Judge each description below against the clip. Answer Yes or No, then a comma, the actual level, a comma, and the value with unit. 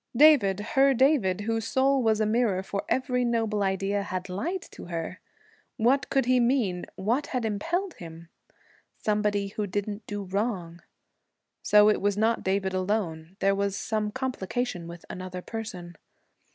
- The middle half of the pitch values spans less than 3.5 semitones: No, average, 4.3 semitones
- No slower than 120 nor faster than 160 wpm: Yes, average, 150 wpm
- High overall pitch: Yes, high, 210 Hz